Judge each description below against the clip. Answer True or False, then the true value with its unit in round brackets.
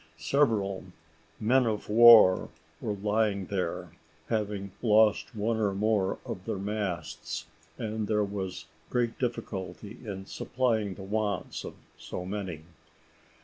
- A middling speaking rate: False (120 wpm)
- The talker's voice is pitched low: True (105 Hz)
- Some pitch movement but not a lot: False (2.3 semitones)